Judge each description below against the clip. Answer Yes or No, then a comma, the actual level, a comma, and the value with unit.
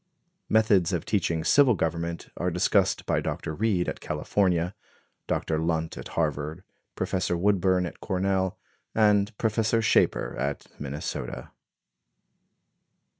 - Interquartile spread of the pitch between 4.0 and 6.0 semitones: No, average, 3.6 semitones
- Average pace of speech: No, slow, 115 wpm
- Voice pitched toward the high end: No, very low, 90 Hz